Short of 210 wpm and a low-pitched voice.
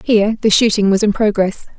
No: average, 200 wpm; high, 210 Hz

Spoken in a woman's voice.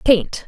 Yes: female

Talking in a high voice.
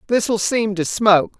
Yes: high, 210 Hz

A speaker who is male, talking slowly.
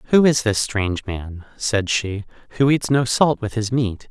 No: male; fast, 205 wpm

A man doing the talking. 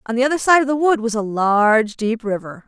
No: female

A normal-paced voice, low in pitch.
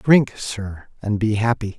Yes: average, 170 wpm; low, 110 Hz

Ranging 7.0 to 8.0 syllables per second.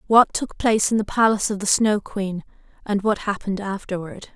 No: 5.6 syllables/s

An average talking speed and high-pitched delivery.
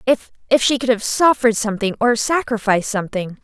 Yes: average, 155 wpm; high, 230 Hz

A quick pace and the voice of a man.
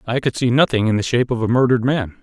Yes: fast, 295 wpm; male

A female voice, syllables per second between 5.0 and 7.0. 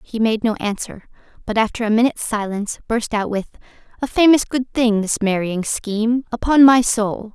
Yes: female; 5.2 syllables/s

